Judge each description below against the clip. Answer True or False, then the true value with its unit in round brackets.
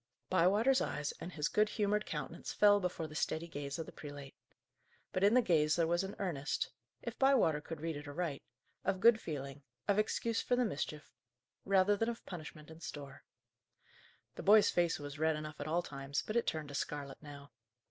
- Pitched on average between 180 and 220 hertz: False (165 Hz)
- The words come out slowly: False (195 wpm)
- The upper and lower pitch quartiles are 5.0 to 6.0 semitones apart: True (5.6 semitones)